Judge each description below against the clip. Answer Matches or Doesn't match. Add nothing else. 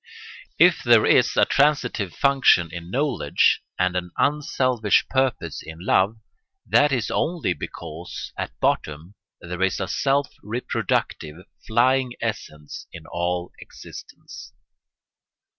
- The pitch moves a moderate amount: Doesn't match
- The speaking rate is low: Matches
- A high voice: Doesn't match